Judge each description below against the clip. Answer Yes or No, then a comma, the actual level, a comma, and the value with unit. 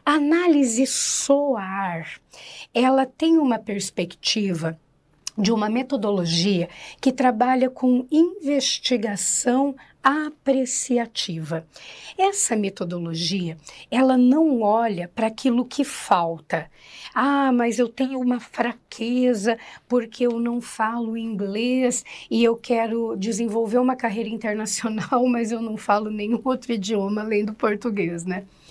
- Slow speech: Yes, slow, 110 wpm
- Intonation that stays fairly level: No, average, 3.7 semitones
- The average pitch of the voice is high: Yes, high, 235 Hz